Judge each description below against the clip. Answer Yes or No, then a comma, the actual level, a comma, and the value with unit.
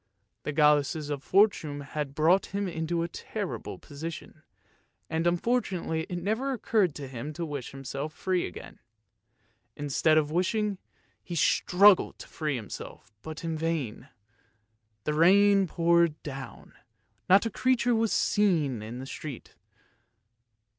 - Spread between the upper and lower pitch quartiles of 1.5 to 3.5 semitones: No, average, 4.7 semitones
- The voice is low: No, medium, 165 Hz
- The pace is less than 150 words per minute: Yes, average, 140 wpm